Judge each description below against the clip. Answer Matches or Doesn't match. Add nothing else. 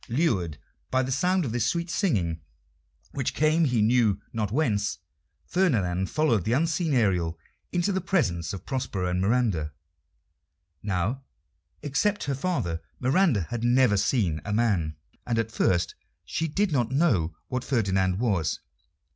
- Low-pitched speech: Matches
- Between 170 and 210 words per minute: Doesn't match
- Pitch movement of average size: Doesn't match